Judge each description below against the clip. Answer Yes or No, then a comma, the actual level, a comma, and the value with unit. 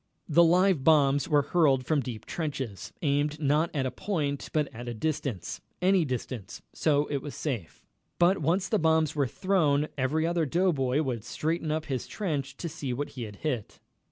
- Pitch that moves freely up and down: No, average, 3.4 semitones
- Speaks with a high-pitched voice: No, medium, 150 Hz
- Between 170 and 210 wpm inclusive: Yes, average, 185 wpm